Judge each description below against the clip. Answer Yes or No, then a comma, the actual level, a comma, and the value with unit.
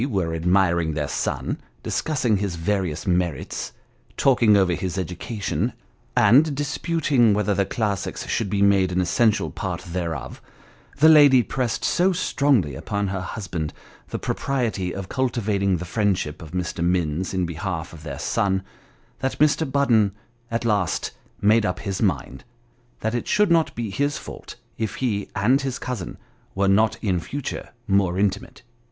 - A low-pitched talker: Yes, low, 100 Hz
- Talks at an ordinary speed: Yes, average, 155 wpm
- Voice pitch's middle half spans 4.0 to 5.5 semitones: Yes, average, 5.0 semitones